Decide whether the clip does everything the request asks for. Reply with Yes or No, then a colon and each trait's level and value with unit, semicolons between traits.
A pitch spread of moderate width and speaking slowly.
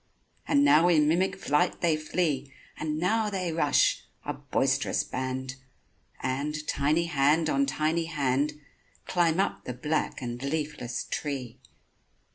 Yes: average, 3.4 semitones; slow, 130 wpm